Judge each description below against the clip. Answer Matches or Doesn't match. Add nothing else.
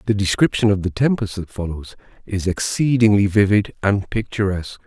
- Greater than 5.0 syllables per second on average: Matches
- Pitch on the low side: Matches